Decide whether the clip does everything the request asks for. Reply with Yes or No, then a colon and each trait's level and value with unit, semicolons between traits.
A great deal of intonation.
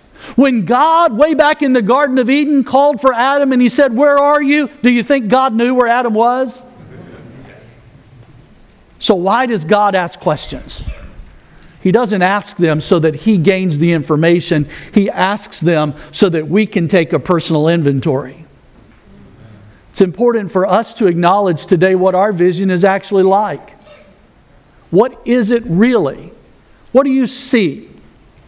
Yes: wide, 7.3 semitones